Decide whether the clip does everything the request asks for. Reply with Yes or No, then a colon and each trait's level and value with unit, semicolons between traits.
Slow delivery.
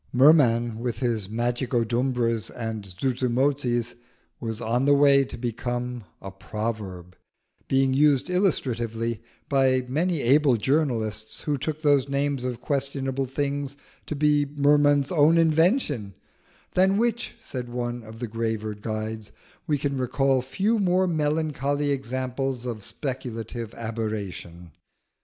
Yes: slow, 120 wpm